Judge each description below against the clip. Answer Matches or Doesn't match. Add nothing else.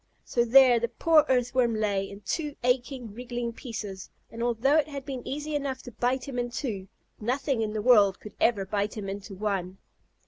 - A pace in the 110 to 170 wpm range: Doesn't match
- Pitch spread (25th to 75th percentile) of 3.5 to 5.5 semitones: Matches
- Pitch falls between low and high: Doesn't match